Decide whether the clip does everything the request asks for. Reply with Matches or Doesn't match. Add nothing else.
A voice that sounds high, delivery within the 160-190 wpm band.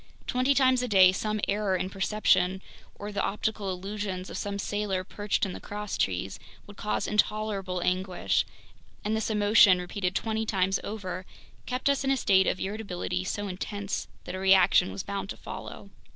Matches